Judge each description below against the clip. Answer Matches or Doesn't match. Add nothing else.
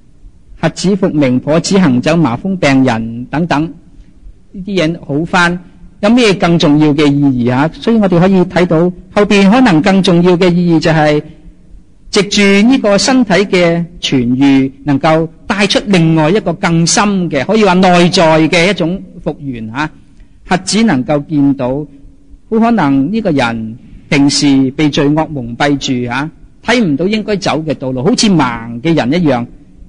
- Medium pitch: Matches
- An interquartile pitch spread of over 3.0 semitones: Matches